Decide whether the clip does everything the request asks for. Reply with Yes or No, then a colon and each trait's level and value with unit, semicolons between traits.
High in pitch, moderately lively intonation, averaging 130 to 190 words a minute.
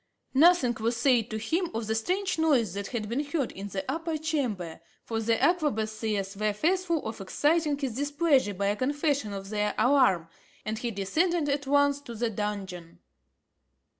No: high, 240 Hz; wide, 5.9 semitones; average, 170 wpm